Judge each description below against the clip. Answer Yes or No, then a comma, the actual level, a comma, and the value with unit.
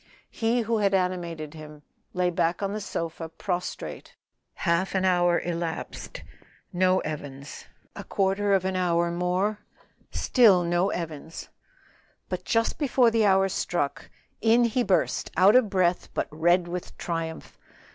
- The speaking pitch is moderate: Yes, medium, 180 Hz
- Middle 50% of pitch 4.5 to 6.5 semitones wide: No, average, 3.0 semitones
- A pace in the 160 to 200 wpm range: No, average, 140 wpm